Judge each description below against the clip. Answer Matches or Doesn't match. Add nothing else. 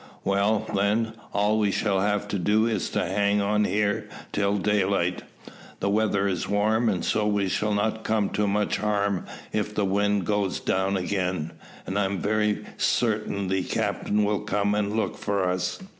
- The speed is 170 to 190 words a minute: Matches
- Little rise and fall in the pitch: Matches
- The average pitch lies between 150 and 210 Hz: Doesn't match